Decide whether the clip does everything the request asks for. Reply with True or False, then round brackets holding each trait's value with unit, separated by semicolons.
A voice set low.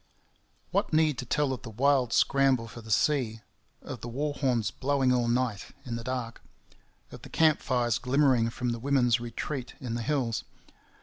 True (125 Hz)